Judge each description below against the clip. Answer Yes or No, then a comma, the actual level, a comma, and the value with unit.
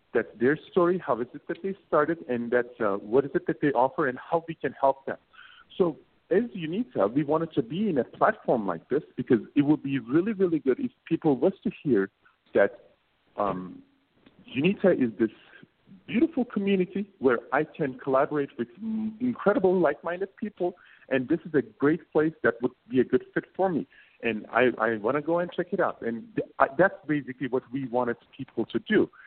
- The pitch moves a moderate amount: No, wide, 6.2 semitones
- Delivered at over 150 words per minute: Yes, average, 200 wpm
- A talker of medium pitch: Yes, medium, 155 Hz